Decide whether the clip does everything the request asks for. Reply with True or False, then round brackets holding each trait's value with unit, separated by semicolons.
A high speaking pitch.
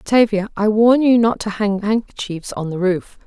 True (210 Hz)